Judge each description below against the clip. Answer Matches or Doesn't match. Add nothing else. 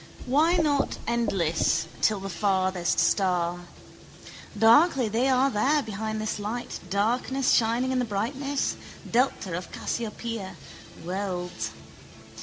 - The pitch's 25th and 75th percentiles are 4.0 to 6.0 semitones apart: Matches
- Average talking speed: Doesn't match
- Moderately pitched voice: Doesn't match